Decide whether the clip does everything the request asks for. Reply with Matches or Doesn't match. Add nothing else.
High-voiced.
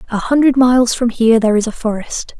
Matches